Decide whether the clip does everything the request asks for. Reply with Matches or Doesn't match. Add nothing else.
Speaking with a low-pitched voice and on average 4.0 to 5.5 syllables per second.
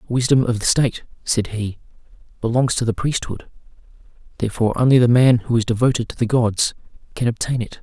Doesn't match